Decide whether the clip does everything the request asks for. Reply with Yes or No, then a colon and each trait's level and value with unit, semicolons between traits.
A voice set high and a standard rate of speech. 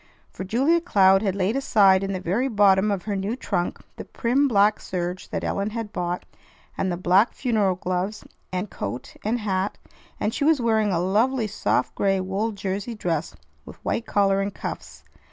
Yes: high, 200 Hz; average, 185 wpm